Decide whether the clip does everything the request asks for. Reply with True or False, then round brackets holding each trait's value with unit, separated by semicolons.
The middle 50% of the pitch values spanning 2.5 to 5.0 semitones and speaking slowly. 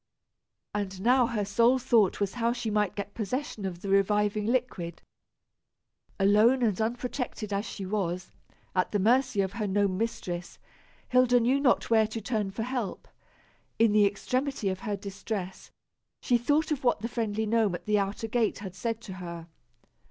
False (3.2 semitones; 170 wpm)